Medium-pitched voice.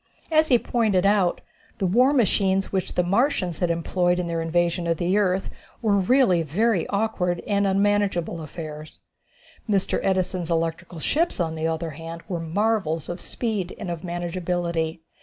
Yes: medium, 180 Hz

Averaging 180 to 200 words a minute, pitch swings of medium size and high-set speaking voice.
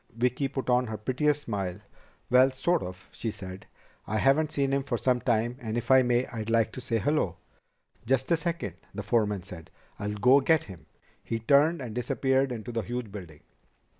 No: average, 195 wpm; average, 4.1 semitones; low, 120 Hz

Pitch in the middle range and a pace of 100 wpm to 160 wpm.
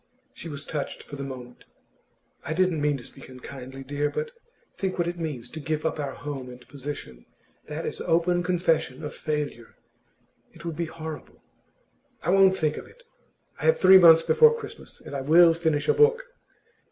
No: medium, 155 Hz; average, 185 wpm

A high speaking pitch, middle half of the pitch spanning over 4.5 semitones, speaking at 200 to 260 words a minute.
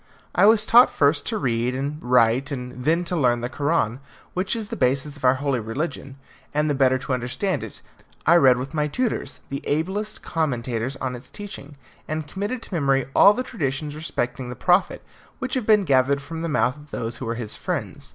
No: medium, 140 Hz; average, 4.9 semitones; fast, 205 wpm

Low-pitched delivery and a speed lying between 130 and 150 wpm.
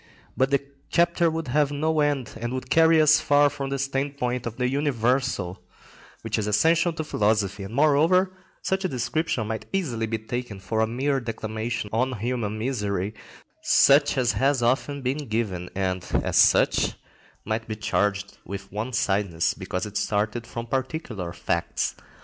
No: low, 120 Hz; average, 160 wpm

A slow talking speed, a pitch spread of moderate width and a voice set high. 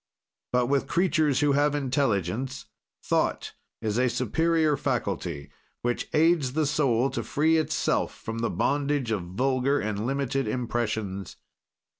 No: slow, 130 wpm; average, 4.5 semitones; low, 130 Hz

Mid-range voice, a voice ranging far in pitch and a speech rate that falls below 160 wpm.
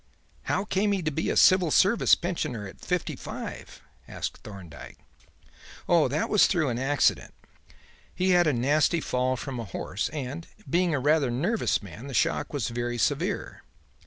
No: medium, 145 Hz; wide, 6.2 semitones; average, 165 wpm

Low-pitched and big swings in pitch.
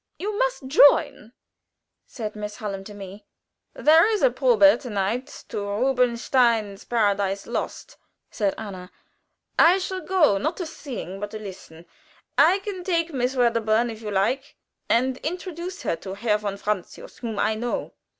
No: high, 235 Hz; wide, 7.1 semitones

